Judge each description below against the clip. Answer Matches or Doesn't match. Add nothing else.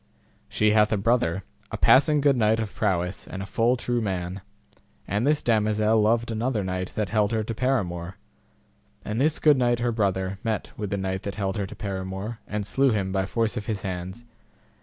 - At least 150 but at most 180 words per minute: Doesn't match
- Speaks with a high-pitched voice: Doesn't match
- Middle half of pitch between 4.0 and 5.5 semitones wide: Doesn't match